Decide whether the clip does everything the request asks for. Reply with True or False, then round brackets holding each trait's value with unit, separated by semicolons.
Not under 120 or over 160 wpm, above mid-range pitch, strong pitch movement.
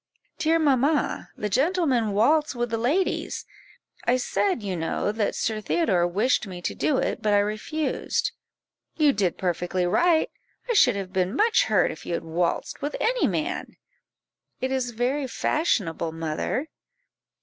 True (155 wpm; 240 Hz; 8.1 semitones)